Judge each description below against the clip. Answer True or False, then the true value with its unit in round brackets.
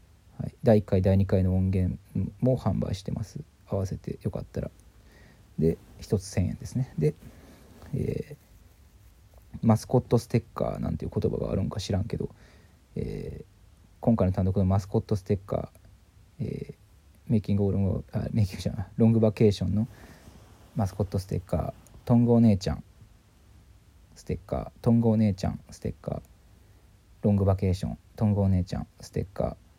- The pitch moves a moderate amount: True (3.0 semitones)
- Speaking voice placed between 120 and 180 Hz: False (100 Hz)